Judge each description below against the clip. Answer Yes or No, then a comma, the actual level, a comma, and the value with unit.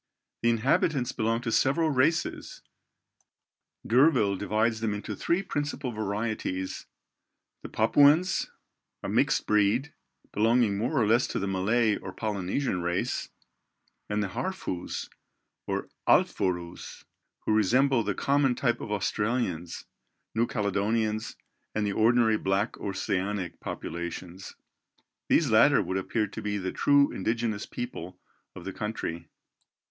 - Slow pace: Yes, slow, 120 wpm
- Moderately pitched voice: No, low, 110 Hz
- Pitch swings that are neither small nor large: Yes, average, 3.9 semitones